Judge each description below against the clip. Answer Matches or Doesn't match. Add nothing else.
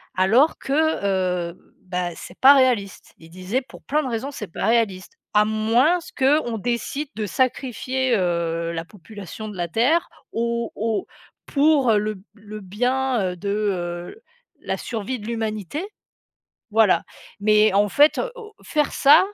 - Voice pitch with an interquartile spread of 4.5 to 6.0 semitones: Matches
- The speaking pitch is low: Doesn't match